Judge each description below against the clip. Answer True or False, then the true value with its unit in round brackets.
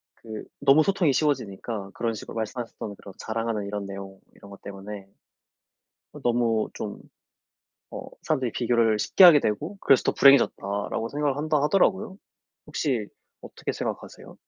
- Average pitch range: False (5.8 semitones)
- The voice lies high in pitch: False (115 Hz)